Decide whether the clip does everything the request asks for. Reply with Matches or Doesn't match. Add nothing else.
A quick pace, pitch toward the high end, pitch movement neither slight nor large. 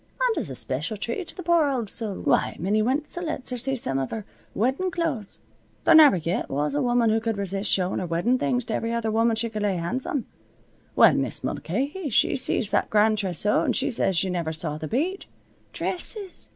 Doesn't match